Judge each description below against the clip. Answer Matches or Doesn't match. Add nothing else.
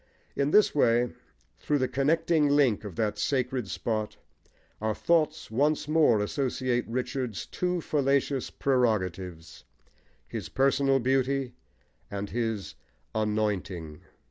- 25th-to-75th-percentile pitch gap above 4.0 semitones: Matches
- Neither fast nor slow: Doesn't match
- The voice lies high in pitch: Doesn't match